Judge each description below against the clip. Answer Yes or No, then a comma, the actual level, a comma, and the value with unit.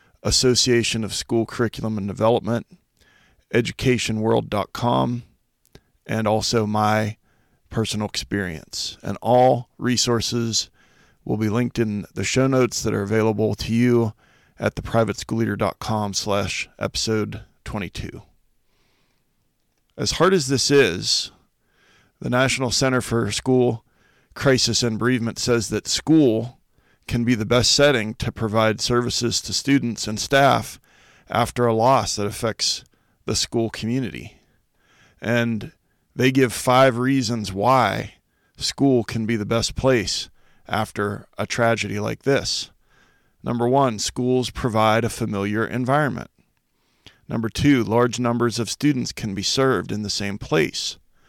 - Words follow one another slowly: Yes, slow, 125 wpm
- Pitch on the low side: Yes, low, 115 Hz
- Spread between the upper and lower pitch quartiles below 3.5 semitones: Yes, average, 2.7 semitones